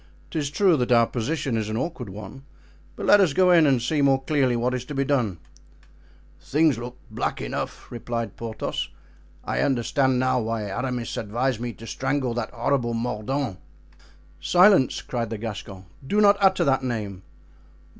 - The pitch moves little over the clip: No, average, 3.7 semitones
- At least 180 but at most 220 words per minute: No, average, 165 wpm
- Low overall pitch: Yes, low, 125 Hz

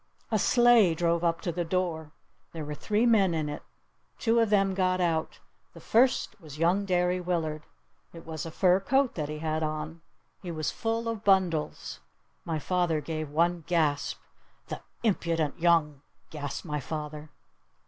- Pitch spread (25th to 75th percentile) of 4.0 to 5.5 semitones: No, average, 3.4 semitones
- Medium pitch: Yes, medium, 170 Hz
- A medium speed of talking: Yes, average, 175 wpm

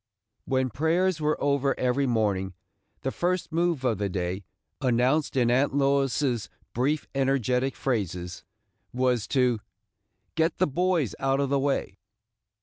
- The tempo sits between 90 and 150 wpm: Yes, slow, 135 wpm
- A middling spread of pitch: Yes, average, 3.3 semitones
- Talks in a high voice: No, low, 135 Hz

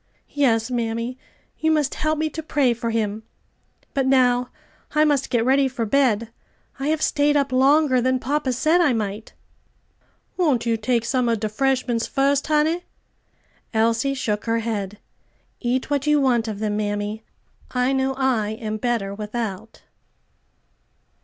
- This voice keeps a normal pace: Yes, average, 155 wpm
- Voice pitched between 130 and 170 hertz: No, very high, 250 Hz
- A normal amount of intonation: Yes, average, 3.7 semitones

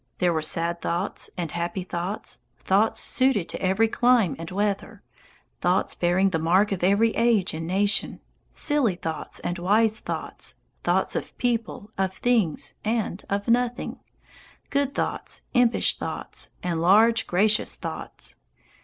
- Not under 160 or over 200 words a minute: No, average, 140 wpm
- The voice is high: Yes, high, 200 Hz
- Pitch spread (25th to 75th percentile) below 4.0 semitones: No, average, 4.4 semitones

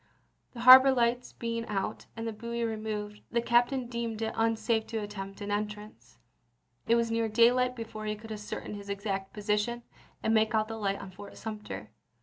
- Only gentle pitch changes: Yes, narrow, 2.0 semitones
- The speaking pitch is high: Yes, high, 220 Hz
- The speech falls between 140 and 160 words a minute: No, average, 185 wpm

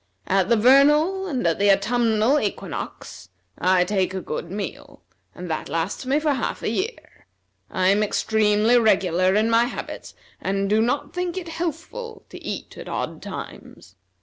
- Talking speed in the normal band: Yes, average, 165 wpm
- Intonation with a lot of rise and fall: Yes, wide, 6.9 semitones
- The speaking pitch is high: Yes, high, 220 Hz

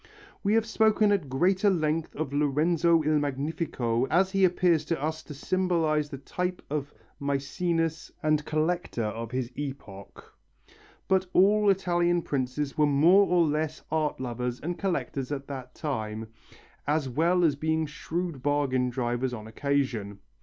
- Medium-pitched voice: Yes, medium, 150 Hz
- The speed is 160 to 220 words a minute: No, average, 145 wpm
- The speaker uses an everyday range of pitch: Yes, average, 4.5 semitones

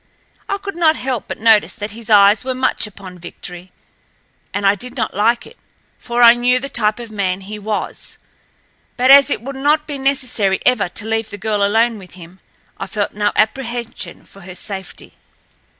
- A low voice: No, high, 220 Hz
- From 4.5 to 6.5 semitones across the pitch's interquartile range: No, average, 3.9 semitones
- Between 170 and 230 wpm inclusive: Yes, average, 190 wpm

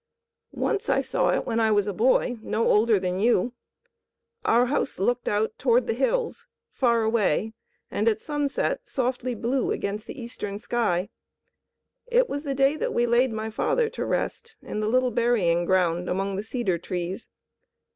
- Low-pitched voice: No, high, 230 Hz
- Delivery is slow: No, average, 170 wpm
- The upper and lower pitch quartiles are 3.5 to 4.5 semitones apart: Yes, average, 3.8 semitones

